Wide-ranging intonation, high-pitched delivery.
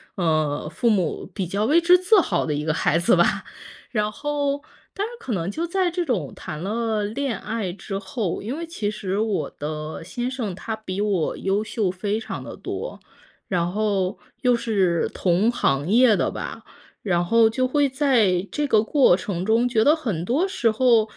Yes: wide, 5.7 semitones; high, 215 Hz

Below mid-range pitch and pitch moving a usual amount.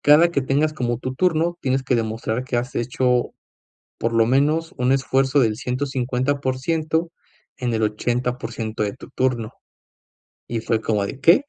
Yes: low, 130 Hz; average, 3.2 semitones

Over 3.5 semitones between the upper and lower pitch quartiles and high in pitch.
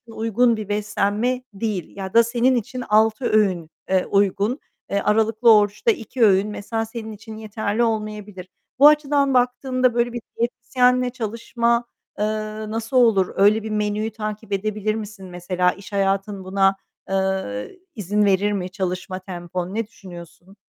No: average, 3.1 semitones; high, 215 Hz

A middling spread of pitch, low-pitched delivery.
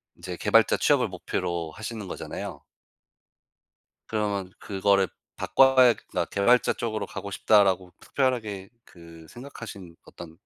Yes: average, 4.0 semitones; low, 100 Hz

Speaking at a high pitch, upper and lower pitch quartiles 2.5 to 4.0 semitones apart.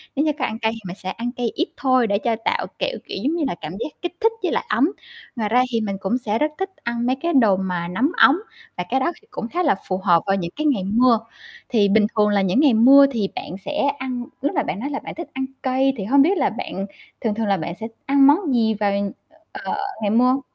No: high, 240 Hz; wide, 5.4 semitones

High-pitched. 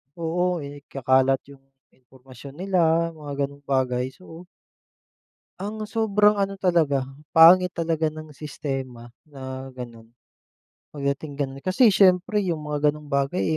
No: medium, 150 Hz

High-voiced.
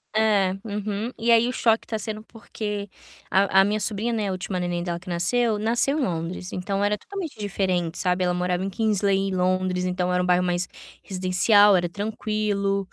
Yes: high, 195 Hz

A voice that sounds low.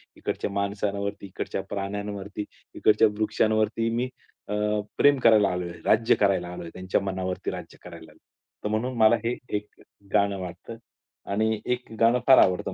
Yes: low, 105 Hz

